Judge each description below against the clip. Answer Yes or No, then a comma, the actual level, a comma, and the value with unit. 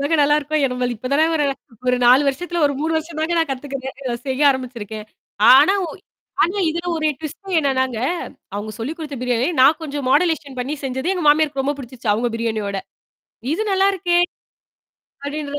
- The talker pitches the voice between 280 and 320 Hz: Yes, very high, 285 Hz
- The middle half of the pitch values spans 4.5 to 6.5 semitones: No, average, 3.9 semitones